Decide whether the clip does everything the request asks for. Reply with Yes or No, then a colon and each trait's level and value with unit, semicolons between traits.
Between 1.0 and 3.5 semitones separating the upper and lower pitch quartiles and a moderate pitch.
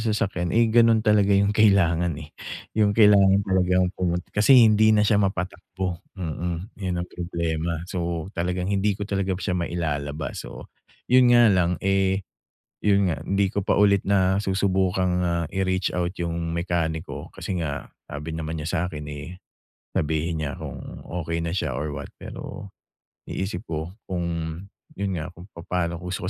No: average, 2.8 semitones; very low, 90 Hz